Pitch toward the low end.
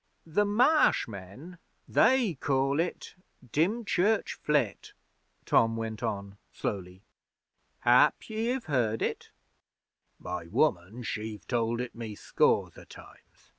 Yes: low, 125 Hz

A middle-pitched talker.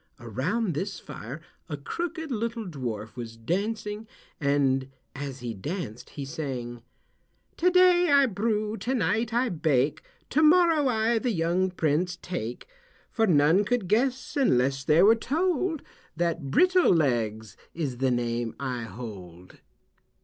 Yes: medium, 170 Hz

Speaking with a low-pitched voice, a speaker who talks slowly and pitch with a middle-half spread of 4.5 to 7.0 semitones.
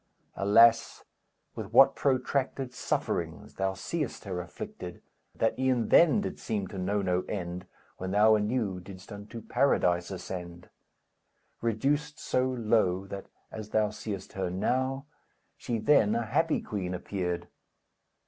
Yes: low, 105 Hz; slow, 130 wpm; average, 5.1 semitones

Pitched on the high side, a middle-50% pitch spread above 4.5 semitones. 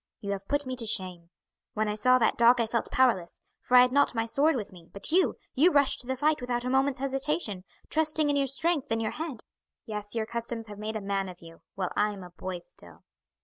Yes: high, 235 Hz; average, 5.1 semitones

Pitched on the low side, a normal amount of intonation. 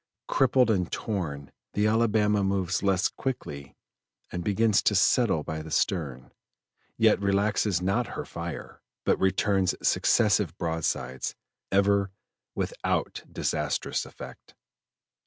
Yes: low, 100 Hz; average, 3.9 semitones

